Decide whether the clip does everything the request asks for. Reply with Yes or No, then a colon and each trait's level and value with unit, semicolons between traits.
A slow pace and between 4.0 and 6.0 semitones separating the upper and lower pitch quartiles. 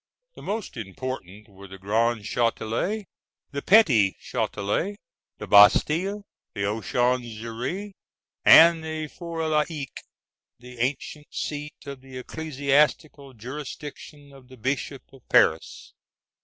Yes: slow, 110 wpm; average, 5.2 semitones